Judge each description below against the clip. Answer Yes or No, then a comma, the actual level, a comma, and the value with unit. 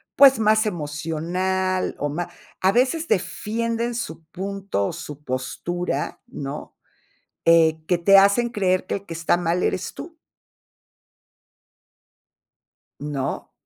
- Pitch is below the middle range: No, medium, 185 Hz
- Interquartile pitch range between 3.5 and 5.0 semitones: Yes, average, 4.7 semitones